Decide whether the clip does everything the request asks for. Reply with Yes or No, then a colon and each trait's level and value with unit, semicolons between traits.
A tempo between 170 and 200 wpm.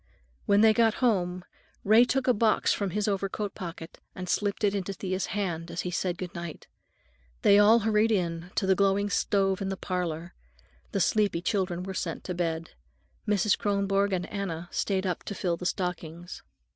Yes: average, 180 wpm